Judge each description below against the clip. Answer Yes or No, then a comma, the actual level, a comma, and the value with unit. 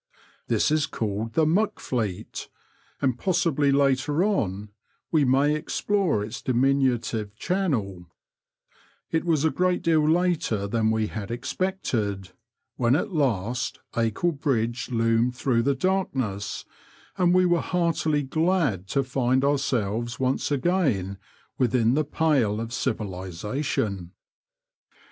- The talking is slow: Yes, slow, 120 wpm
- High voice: No, low, 130 Hz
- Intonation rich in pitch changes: Yes, wide, 6.2 semitones